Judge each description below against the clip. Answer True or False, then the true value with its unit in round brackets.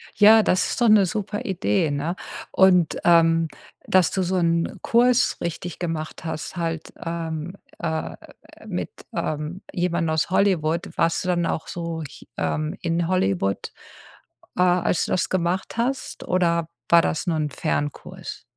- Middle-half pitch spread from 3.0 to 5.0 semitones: False (2.4 semitones)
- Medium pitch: True (170 Hz)